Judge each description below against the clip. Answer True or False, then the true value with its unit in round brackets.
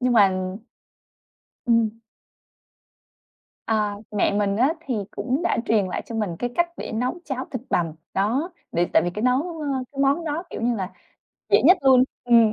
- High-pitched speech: True (235 Hz)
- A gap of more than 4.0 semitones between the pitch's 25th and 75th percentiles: True (4.5 semitones)